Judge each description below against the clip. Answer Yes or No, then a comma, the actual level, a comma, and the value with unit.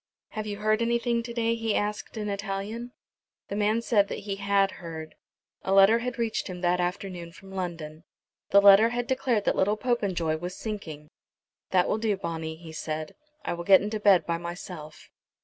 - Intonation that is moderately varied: Yes, average, 3.9 semitones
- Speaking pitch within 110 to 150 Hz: No, high, 200 Hz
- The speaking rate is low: No, average, 185 wpm